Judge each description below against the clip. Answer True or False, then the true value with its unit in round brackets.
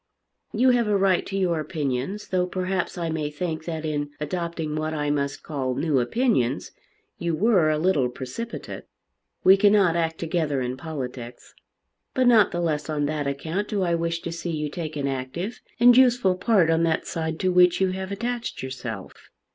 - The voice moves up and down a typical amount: True (4.2 semitones)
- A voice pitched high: False (165 Hz)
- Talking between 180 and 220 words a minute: True (185 wpm)